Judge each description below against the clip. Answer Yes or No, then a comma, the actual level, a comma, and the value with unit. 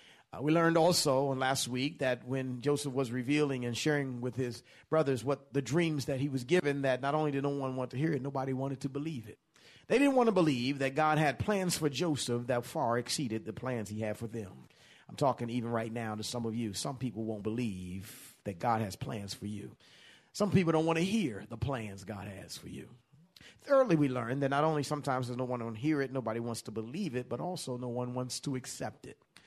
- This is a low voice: Yes, low, 130 Hz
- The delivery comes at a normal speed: No, fast, 235 wpm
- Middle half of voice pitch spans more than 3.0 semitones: Yes, average, 3.8 semitones